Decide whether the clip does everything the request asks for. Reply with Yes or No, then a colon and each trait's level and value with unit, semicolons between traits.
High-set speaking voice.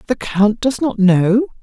Yes: high, 220 Hz